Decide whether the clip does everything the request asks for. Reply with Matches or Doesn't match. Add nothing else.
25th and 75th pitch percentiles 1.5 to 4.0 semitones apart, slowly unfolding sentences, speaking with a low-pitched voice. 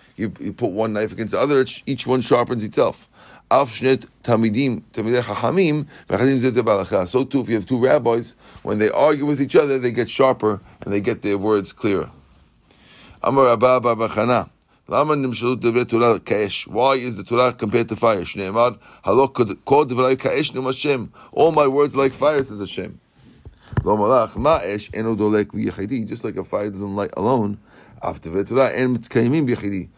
Matches